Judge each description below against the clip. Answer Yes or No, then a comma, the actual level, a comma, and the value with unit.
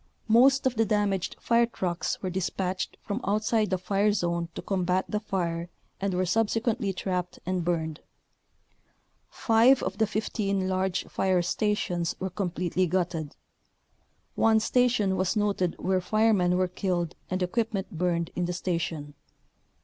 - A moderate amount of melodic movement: Yes, average, 3.0 semitones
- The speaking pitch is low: No, high, 190 Hz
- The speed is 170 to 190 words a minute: No, average, 145 wpm